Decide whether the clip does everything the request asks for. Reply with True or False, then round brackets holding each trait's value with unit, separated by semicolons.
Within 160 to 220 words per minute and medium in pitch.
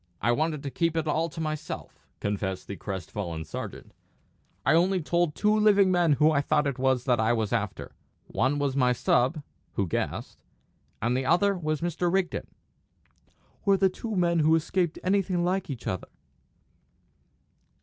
True (170 wpm; 155 Hz)